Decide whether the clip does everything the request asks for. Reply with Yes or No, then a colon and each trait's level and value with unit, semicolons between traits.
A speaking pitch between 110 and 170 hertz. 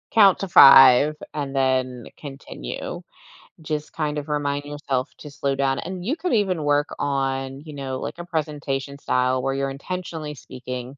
Yes: medium, 140 Hz